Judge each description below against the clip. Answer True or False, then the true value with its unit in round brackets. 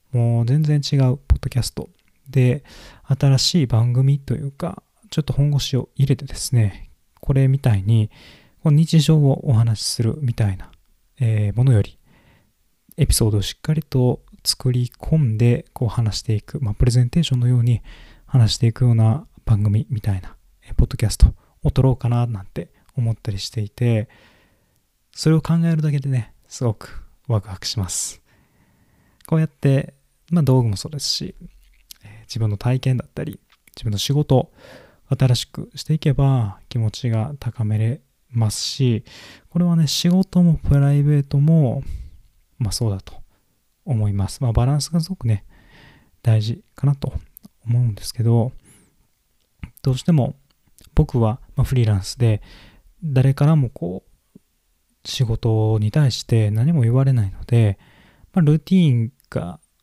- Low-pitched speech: True (125 Hz)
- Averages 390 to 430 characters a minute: False (290 characters per minute)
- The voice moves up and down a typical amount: True (4.5 semitones)